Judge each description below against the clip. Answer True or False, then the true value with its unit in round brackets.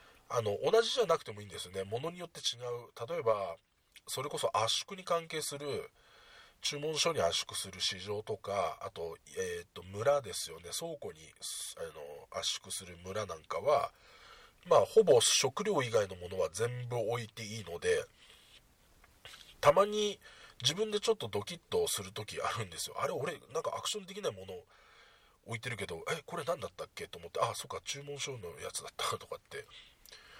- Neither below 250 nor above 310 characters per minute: False (345 characters per minute)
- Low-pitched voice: False (165 Hz)